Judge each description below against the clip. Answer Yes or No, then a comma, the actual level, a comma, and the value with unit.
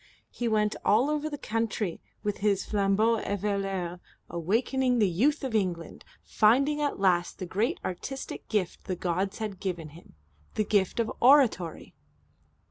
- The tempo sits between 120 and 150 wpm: Yes, average, 145 wpm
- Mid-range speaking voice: No, high, 210 Hz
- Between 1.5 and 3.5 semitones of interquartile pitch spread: No, average, 4.0 semitones